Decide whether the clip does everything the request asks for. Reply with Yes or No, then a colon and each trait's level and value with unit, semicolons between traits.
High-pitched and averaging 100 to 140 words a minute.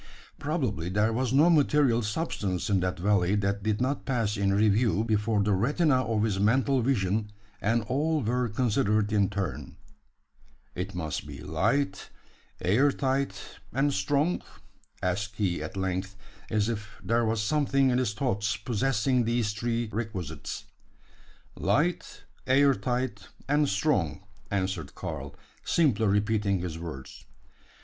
No: low, 110 Hz; slow, 135 wpm